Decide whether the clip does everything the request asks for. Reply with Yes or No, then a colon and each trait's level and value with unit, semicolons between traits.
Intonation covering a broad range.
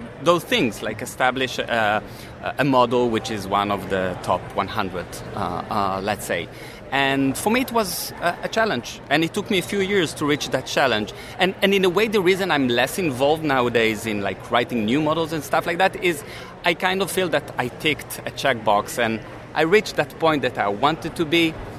Yes: wide, 6.8 semitones